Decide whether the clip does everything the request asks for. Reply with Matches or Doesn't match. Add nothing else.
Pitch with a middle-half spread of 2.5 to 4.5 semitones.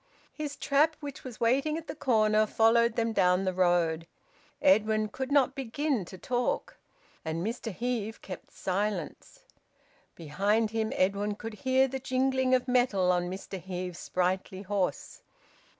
Doesn't match